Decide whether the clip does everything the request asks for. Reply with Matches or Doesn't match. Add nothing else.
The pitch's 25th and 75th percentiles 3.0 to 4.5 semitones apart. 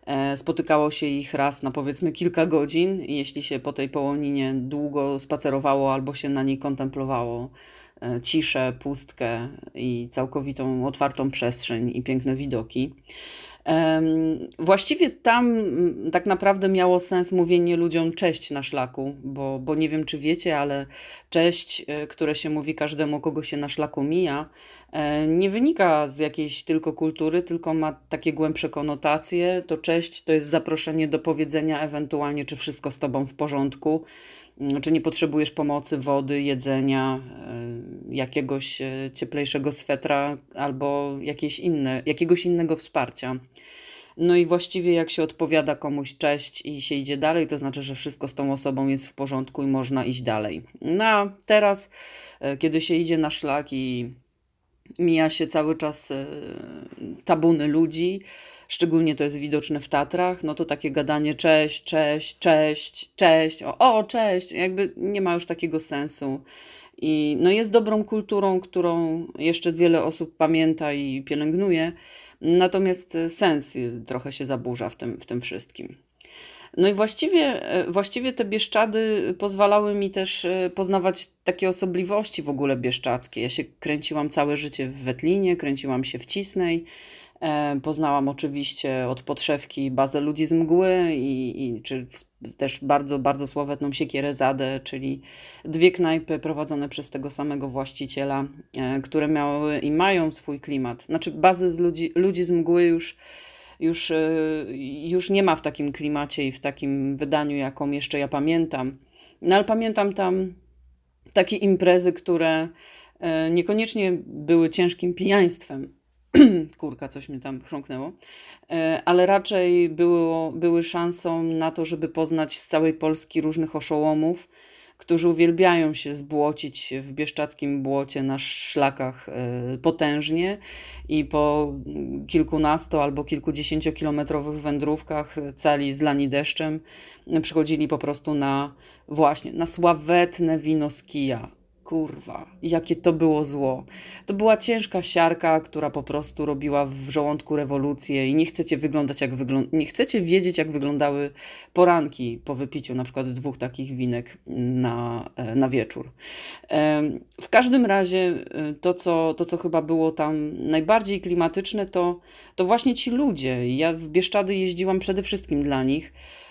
Matches